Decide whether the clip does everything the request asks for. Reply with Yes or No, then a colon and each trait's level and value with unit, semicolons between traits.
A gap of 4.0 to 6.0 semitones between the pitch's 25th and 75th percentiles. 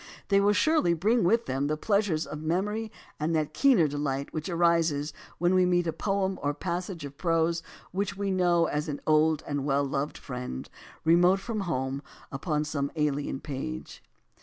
Yes: average, 4.4 semitones